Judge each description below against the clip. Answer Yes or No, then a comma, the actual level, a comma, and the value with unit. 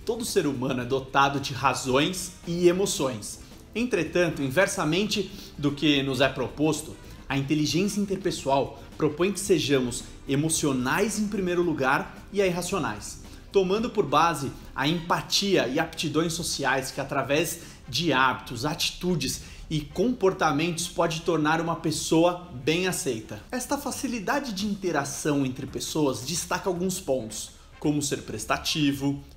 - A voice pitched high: No, medium, 160 Hz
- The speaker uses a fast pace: No, average, 125 wpm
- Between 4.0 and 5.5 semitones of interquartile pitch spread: Yes, average, 4.9 semitones